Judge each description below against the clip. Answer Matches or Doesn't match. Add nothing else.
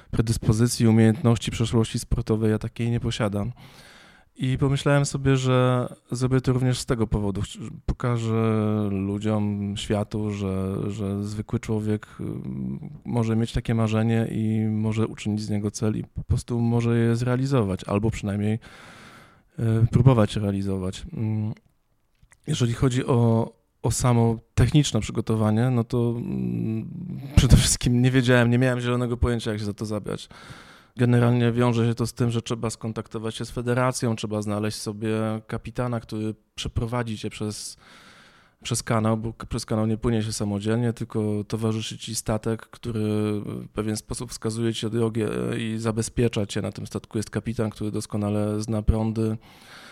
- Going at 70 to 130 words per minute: Doesn't match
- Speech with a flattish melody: Matches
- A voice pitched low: Matches